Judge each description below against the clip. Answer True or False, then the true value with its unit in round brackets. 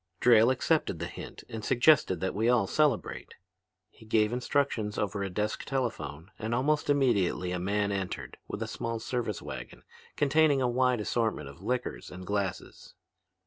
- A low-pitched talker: True (110 Hz)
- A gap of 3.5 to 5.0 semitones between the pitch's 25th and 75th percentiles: True (4.5 semitones)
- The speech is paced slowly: False (160 wpm)